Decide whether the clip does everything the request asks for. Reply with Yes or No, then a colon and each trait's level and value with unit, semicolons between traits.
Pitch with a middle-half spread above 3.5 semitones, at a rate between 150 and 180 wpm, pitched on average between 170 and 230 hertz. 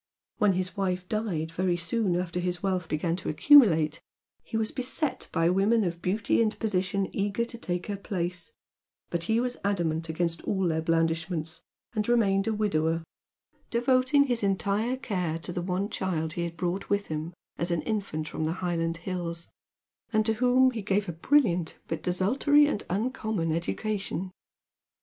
Yes: average, 4.3 semitones; average, 170 wpm; medium, 185 Hz